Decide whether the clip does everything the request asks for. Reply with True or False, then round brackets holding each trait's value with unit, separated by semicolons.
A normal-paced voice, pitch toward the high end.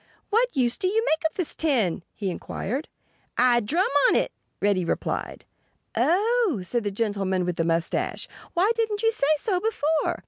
True (170 wpm; 285 Hz)